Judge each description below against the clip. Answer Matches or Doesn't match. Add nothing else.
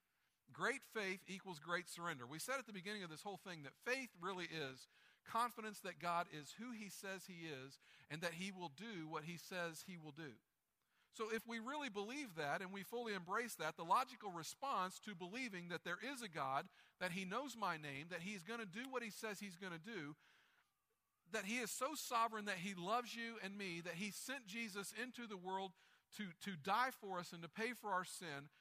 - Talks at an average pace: Doesn't match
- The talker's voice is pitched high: Matches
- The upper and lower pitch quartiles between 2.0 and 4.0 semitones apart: Doesn't match